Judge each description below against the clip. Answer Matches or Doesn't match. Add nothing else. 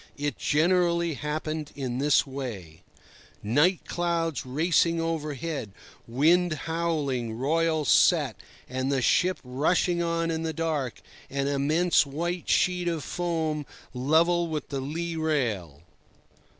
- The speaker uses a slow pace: Matches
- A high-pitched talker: Doesn't match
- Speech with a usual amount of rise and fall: Matches